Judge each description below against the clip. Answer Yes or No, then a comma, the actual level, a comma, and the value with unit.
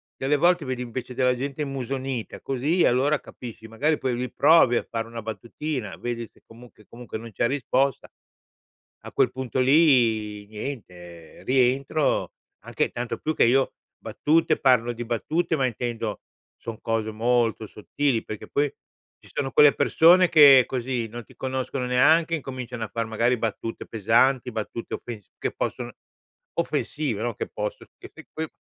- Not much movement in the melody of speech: No, average, 3.3 semitones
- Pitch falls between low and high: No, low, 125 Hz